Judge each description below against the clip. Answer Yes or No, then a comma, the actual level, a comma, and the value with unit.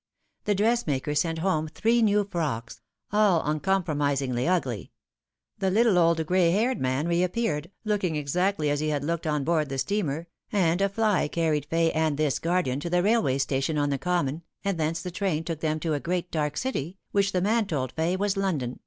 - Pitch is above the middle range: No, medium, 165 Hz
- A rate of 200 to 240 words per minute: Yes, fast, 205 wpm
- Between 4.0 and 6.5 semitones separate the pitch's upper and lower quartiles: Yes, average, 4.5 semitones